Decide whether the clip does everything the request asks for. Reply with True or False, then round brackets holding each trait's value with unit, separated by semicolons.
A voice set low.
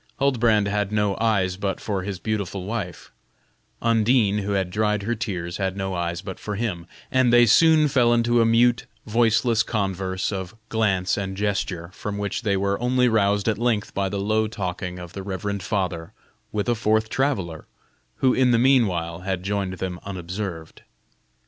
True (100 Hz)